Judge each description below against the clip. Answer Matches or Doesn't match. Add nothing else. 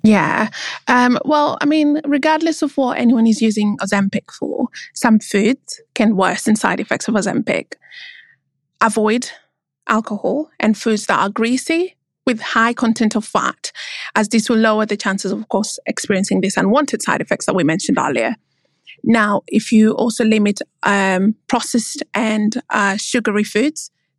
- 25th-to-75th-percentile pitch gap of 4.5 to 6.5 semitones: Doesn't match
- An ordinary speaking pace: Matches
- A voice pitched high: Matches